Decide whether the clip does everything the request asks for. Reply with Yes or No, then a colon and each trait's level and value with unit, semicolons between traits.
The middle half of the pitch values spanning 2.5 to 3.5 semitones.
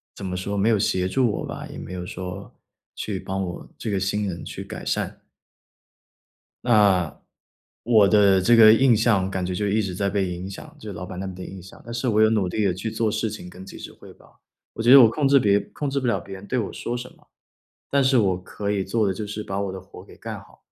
Yes: average, 3.0 semitones